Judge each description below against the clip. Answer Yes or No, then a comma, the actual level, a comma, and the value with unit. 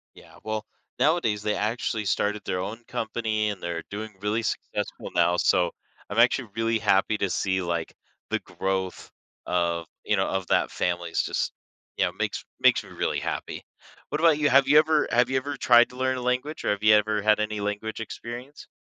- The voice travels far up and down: No, average, 4.1 semitones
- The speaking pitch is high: No, low, 110 Hz